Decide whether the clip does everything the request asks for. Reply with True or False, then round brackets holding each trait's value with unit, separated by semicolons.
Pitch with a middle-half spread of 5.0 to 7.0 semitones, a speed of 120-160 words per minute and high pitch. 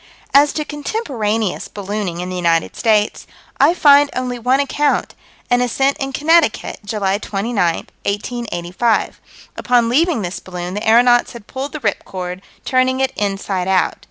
True (5.4 semitones; 150 wpm; 230 Hz)